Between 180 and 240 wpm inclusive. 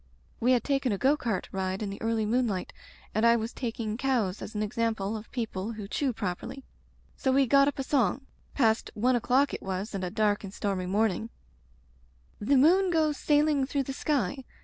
Yes: average, 200 wpm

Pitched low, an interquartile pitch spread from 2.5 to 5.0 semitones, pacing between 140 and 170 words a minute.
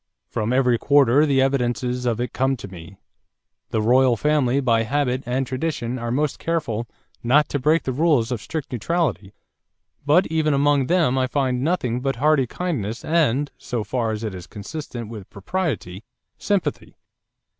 Yes: low, 130 Hz; average, 4.0 semitones; average, 160 wpm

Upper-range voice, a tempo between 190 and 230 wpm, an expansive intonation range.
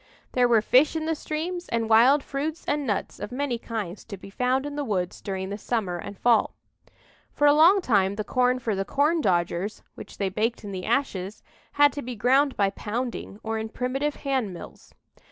Yes: high, 240 Hz; average, 200 wpm; wide, 5.8 semitones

